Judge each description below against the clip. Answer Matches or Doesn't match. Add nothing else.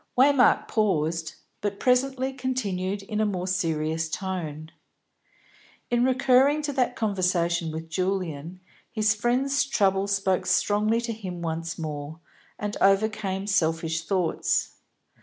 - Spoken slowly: Matches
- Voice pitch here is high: Matches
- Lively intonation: Matches